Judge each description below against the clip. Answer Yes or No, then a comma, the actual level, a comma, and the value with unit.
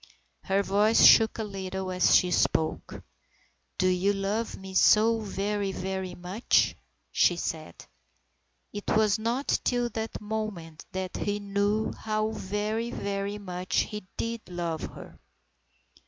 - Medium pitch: No, high, 200 Hz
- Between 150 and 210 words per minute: No, average, 140 wpm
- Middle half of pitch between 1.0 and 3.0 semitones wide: Yes, average, 2.7 semitones